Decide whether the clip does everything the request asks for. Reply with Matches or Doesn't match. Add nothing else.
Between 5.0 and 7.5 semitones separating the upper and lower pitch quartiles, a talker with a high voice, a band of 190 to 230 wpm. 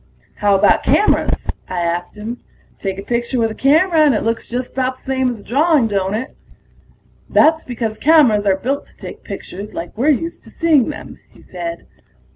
Matches